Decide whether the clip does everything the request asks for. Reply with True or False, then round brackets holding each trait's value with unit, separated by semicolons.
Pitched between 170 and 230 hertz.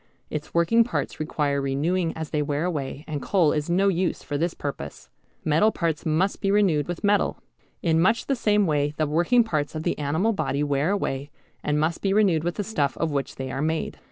False (160 Hz)